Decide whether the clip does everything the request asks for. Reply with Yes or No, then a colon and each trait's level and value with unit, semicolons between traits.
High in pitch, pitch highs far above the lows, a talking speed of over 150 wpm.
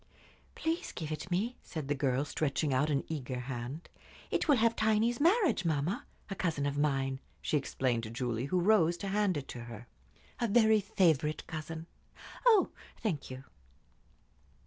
No: medium, 155 Hz; wide, 7.3 semitones; average, 165 wpm